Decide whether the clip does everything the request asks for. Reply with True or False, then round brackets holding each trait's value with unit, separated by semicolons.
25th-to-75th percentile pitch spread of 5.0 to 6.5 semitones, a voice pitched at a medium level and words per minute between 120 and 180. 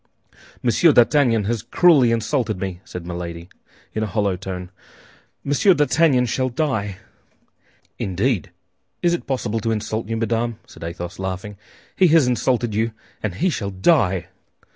False (5.3 semitones; 115 Hz; 140 wpm)